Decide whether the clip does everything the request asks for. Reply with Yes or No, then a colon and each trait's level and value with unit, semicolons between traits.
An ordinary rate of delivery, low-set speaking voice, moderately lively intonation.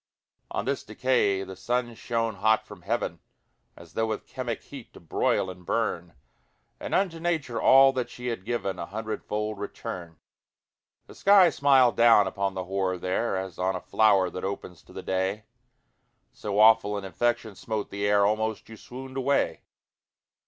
Yes: average, 165 wpm; low, 110 Hz; average, 4.0 semitones